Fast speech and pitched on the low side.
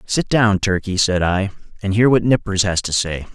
Yes: fast, 215 wpm; low, 100 Hz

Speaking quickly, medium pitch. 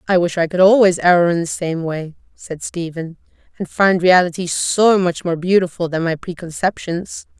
No: average, 180 wpm; medium, 175 Hz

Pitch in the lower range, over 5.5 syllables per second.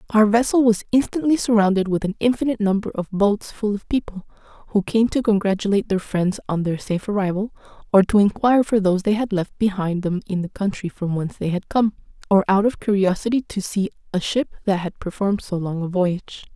No: high, 200 Hz; 6.0 syllables/s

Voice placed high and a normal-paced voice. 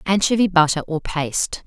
No: medium, 170 Hz; average, 180 wpm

